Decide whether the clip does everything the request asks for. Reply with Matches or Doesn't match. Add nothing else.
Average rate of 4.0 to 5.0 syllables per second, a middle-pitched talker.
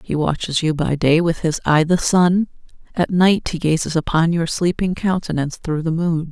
Matches